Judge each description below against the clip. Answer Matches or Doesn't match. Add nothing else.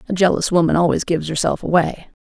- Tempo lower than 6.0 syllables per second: Doesn't match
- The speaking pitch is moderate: Matches